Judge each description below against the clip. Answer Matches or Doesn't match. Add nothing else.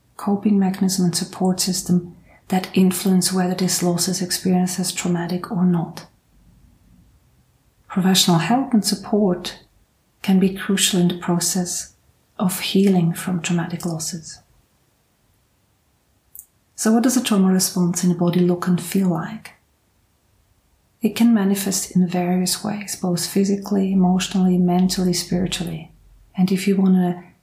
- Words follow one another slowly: Matches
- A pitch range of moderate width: Doesn't match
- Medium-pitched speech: Matches